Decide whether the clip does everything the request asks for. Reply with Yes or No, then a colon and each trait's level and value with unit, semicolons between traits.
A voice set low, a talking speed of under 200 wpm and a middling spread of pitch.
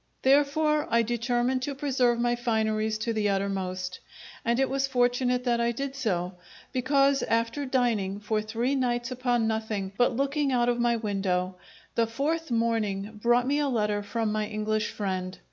No: high, 235 Hz; average, 165 wpm; average, 3.3 semitones